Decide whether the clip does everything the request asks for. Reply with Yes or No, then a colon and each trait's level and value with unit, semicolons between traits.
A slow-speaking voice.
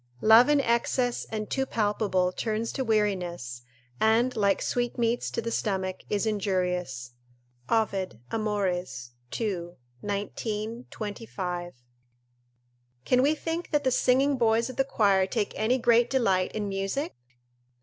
Yes: slow, 130 wpm